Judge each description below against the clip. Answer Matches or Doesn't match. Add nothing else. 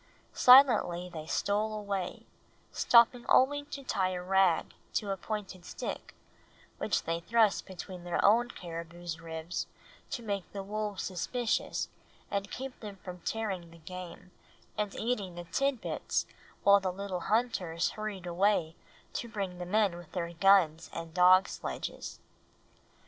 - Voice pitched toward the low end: Doesn't match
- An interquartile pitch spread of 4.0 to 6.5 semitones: Doesn't match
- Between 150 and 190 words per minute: Doesn't match